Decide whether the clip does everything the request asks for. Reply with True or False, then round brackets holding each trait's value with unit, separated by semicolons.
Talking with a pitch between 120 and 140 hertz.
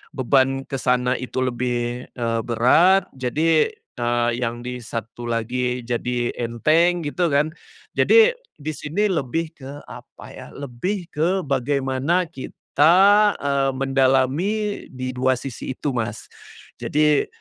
True (135 Hz)